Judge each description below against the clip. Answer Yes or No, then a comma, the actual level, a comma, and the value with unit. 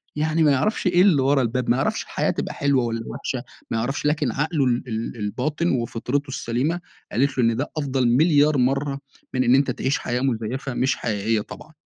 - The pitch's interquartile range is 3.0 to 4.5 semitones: Yes, average, 3.4 semitones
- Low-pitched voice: Yes, low, 130 Hz